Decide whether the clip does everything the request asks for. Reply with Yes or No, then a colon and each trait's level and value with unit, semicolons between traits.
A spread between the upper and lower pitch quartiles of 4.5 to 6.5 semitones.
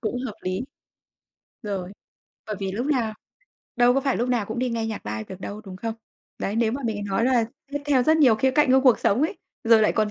No: average, 3.9 semitones